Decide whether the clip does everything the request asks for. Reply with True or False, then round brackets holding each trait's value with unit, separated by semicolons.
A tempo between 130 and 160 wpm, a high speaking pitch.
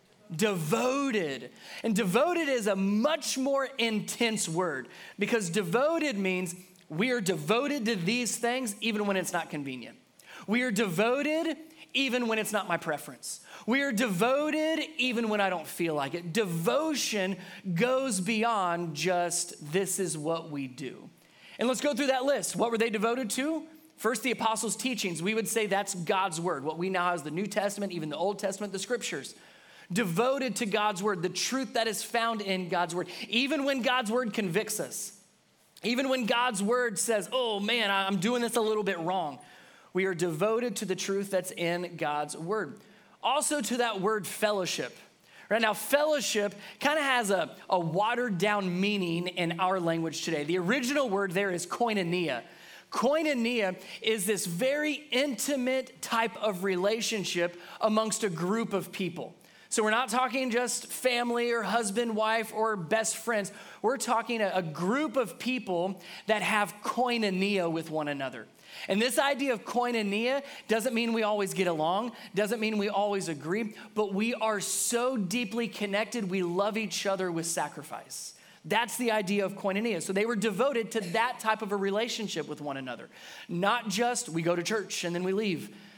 False (170 wpm; 215 Hz)